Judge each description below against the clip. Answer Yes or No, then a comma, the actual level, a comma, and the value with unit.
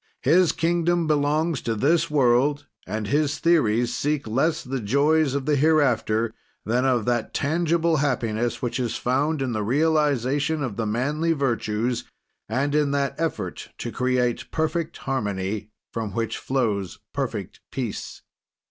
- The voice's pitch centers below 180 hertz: Yes, low, 135 Hz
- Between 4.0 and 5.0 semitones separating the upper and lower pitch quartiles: Yes, average, 4.7 semitones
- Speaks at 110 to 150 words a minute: Yes, average, 140 wpm